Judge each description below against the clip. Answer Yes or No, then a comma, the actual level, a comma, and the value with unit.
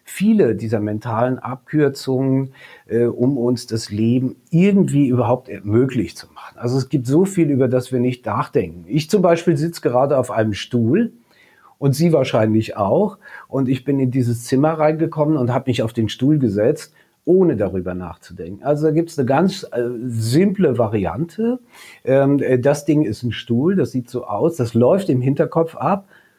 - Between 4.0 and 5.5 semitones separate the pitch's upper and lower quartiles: Yes, average, 4.7 semitones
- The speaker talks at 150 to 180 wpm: Yes, average, 175 wpm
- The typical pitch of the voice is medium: No, low, 130 Hz